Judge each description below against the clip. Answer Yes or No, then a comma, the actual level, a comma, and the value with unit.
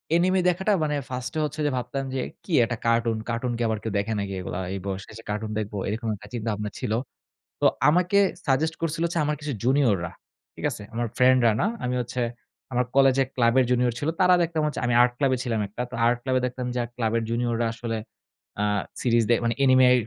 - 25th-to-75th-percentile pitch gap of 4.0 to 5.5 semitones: No, average, 3.2 semitones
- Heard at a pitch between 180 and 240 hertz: No, low, 125 Hz